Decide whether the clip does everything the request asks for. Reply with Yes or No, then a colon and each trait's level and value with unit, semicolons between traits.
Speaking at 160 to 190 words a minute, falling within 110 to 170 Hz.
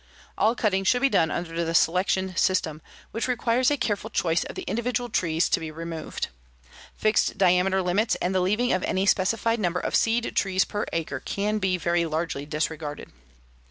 No: average, 180 wpm; medium, 185 Hz